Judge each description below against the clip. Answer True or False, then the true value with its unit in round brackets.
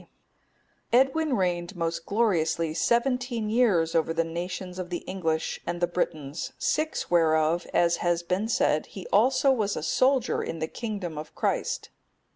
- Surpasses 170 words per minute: False (155 wpm)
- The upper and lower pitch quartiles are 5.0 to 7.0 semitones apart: True (5.5 semitones)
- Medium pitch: True (175 Hz)